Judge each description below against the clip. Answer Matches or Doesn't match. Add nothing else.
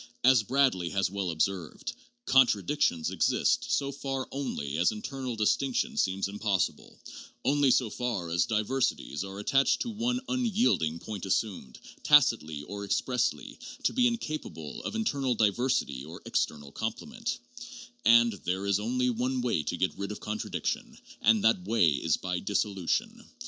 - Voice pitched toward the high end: Doesn't match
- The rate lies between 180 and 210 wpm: Doesn't match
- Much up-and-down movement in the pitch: Matches